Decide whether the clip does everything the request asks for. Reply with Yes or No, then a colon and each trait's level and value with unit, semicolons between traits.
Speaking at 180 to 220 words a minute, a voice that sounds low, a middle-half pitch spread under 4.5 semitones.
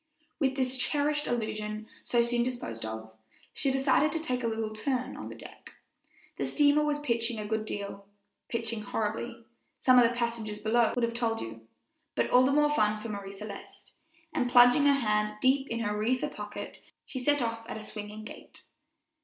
No: average, 185 wpm; high, 235 Hz; average, 3.4 semitones